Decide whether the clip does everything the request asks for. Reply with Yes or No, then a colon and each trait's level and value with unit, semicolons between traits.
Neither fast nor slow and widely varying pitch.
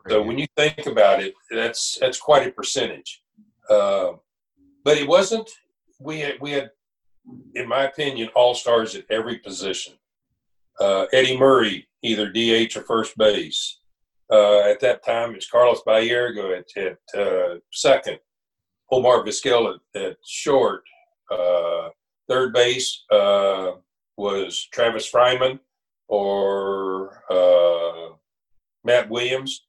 No: slow, 125 wpm; wide, 6.5 semitones